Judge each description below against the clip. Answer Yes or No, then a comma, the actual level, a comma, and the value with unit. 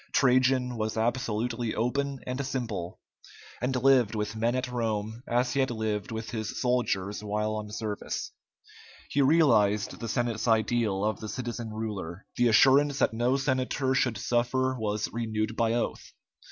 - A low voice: Yes, low, 115 Hz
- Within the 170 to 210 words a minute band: No, average, 155 wpm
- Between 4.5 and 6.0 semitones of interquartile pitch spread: No, average, 2.9 semitones